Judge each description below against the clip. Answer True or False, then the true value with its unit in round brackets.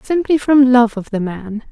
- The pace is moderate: False (210 wpm)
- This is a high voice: True (245 Hz)